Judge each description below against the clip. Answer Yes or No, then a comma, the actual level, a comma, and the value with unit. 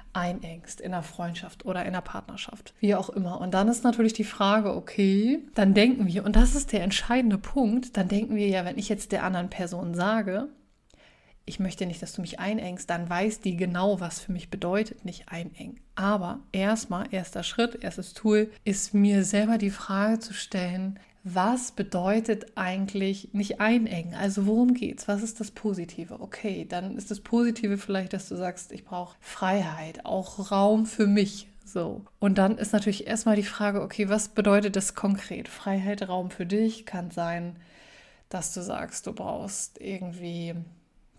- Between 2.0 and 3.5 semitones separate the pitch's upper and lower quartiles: Yes, average, 2.7 semitones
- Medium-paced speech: Yes, average, 175 wpm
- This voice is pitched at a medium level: No, high, 200 Hz